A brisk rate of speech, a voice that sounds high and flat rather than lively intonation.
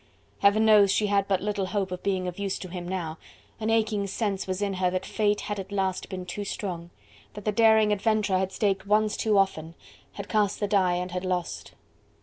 Yes: fast, 215 wpm; high, 195 Hz; narrow, 2.1 semitones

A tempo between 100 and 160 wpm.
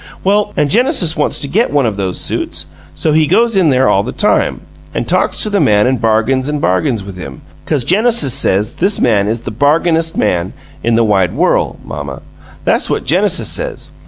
No: average, 200 wpm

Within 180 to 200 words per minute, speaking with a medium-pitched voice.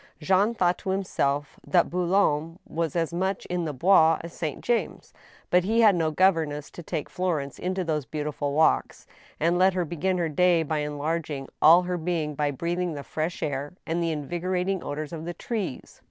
Yes: average, 185 wpm; medium, 170 Hz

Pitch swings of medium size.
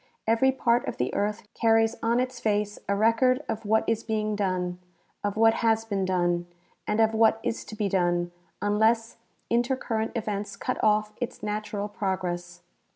No: narrow, 2.1 semitones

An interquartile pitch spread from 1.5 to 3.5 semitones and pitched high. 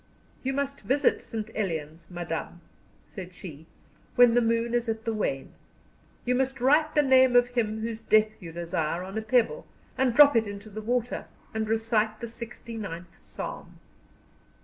No: average, 4.2 semitones; high, 225 Hz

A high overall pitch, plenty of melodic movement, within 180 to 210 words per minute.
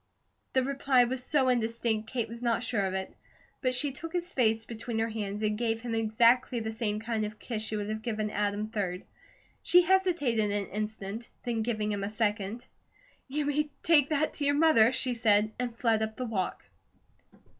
No: high, 225 Hz; average, 3.0 semitones; average, 195 wpm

